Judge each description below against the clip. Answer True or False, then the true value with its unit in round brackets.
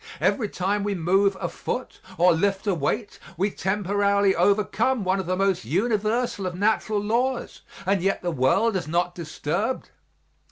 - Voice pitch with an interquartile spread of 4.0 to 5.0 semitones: False (2.7 semitones)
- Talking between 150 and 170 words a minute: True (160 wpm)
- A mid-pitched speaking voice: False (195 Hz)